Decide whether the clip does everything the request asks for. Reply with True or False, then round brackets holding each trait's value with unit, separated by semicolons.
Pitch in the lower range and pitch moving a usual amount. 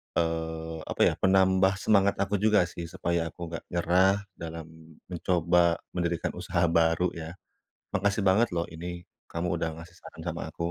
False (85 Hz; 2.3 semitones)